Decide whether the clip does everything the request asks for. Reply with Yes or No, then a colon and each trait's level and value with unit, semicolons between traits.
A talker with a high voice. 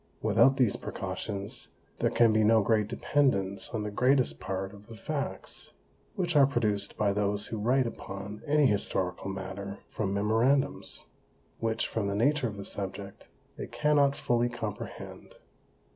No: low, 110 Hz